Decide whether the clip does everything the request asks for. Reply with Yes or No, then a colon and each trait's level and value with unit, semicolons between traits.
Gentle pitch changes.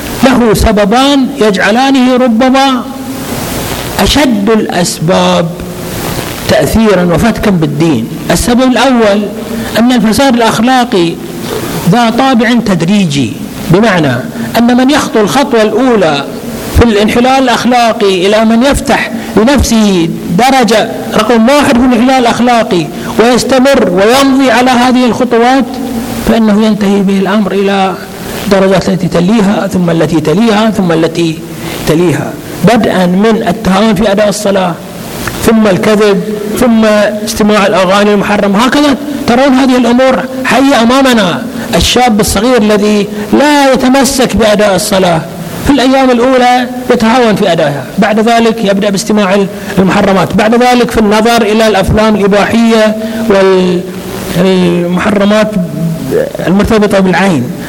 No: average, 4.0 semitones